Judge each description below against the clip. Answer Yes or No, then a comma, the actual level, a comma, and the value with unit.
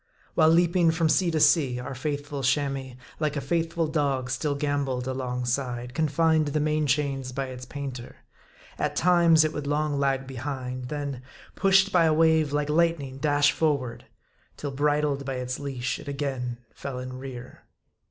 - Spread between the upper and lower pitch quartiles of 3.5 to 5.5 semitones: No, average, 2.9 semitones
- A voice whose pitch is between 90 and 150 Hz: Yes, medium, 140 Hz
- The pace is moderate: Yes, average, 170 wpm